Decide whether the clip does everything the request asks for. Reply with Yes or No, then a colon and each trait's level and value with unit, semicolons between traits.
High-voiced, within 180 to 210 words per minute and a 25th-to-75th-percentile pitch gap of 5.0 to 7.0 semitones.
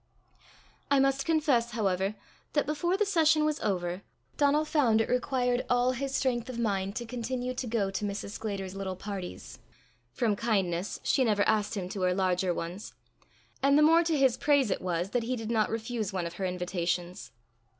Yes: high, 225 Hz; average, 185 wpm; wide, 5.6 semitones